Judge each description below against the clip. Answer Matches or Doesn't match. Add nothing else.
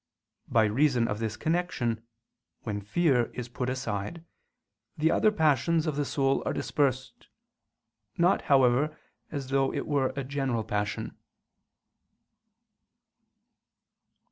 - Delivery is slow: Matches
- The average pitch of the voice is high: Doesn't match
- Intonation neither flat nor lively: Matches